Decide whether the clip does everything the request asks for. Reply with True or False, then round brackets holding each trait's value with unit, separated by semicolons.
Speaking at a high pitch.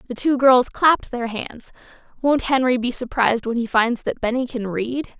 True (245 Hz)